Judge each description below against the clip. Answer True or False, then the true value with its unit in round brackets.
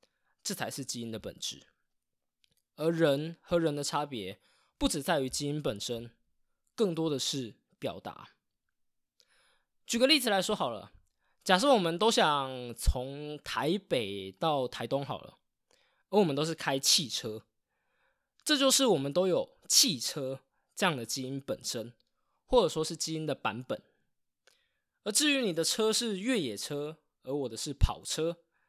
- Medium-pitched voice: True (155 Hz)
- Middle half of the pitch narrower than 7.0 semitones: False (8.0 semitones)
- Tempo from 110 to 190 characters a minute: False (210 characters per minute)